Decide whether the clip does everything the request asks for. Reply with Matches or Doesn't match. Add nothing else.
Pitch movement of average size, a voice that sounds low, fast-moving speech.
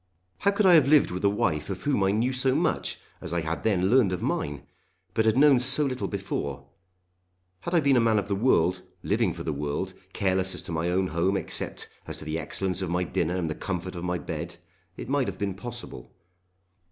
Doesn't match